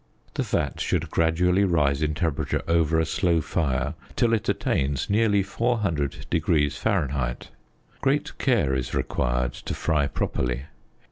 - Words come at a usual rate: No, slow, 130 wpm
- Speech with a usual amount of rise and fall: Yes, average, 4.5 semitones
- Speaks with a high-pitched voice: No, very low, 80 Hz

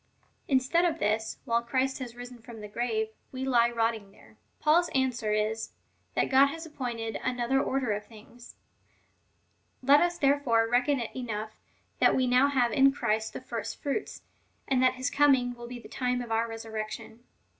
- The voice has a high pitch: Yes, high, 245 Hz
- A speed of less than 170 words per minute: No, average, 180 wpm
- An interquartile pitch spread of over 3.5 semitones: No, average, 3.0 semitones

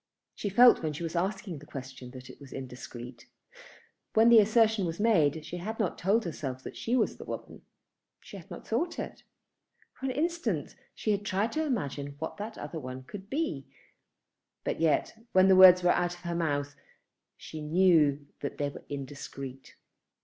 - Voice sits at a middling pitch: Yes, medium, 170 Hz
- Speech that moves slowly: No, average, 185 wpm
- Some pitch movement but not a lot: No, wide, 6.8 semitones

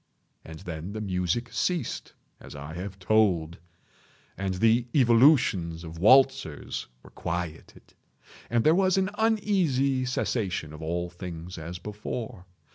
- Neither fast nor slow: No, slow, 130 wpm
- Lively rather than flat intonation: Yes, wide, 7.0 semitones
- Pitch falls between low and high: No, low, 100 Hz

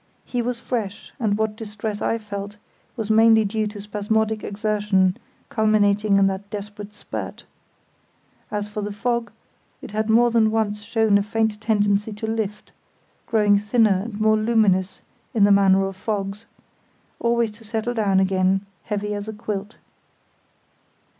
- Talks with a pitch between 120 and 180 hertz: No, high, 210 Hz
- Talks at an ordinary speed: Yes, average, 150 wpm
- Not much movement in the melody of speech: Yes, narrow, 1.5 semitones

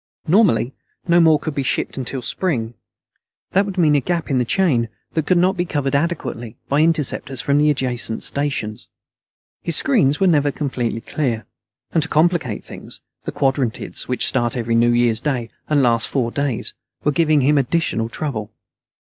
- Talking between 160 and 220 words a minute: Yes, average, 175 wpm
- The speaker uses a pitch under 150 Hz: Yes, medium, 140 Hz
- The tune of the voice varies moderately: Yes, average, 4.8 semitones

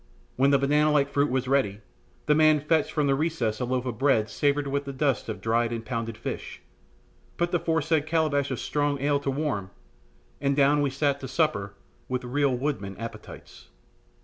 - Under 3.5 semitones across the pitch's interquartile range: Yes, average, 2.9 semitones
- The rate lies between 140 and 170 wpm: No, average, 195 wpm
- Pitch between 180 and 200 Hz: No, medium, 140 Hz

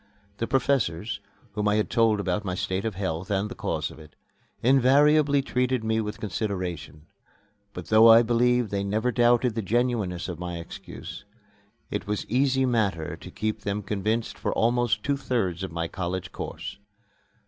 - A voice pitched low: Yes, low, 110 Hz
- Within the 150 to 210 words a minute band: Yes, average, 170 wpm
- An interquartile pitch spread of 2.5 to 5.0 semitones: Yes, average, 4.5 semitones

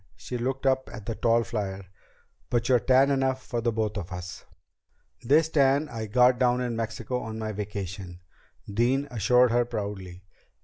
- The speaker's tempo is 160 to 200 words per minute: Yes, average, 165 wpm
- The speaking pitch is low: Yes, low, 115 Hz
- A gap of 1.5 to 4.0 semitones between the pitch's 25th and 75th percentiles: Yes, average, 3.5 semitones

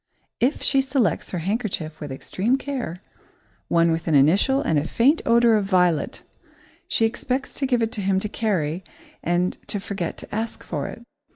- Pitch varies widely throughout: Yes, wide, 5.9 semitones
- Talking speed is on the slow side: No, average, 180 wpm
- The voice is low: No, high, 200 Hz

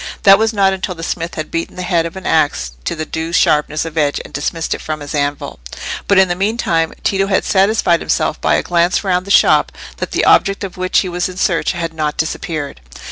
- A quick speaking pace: Yes, fast, 235 wpm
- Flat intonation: No, average, 3.2 semitones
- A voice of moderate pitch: Yes, medium, 170 Hz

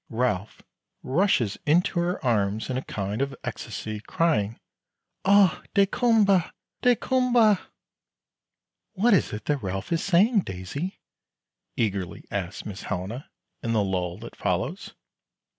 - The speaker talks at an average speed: No, slow, 120 wpm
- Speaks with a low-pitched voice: Yes, low, 130 Hz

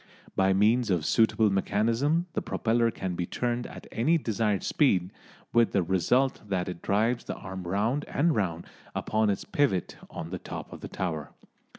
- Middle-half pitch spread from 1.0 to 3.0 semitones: No, average, 4.1 semitones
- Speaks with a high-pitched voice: No, low, 105 Hz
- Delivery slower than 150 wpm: No, average, 175 wpm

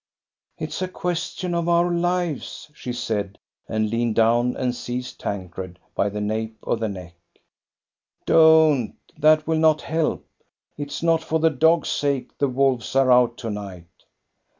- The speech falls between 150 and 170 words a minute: Yes, average, 160 wpm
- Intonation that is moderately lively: No, wide, 6.4 semitones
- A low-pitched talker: Yes, low, 130 Hz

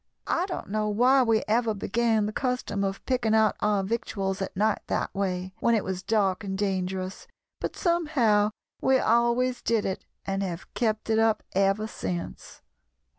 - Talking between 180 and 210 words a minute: No, average, 170 wpm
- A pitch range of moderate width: Yes, average, 3.3 semitones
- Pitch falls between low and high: No, high, 215 Hz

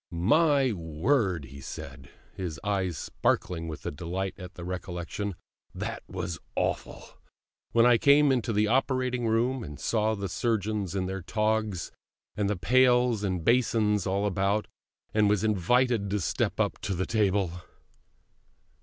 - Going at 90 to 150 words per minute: Yes, average, 145 wpm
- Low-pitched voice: Yes, low, 105 Hz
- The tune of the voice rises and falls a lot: No, average, 4.2 semitones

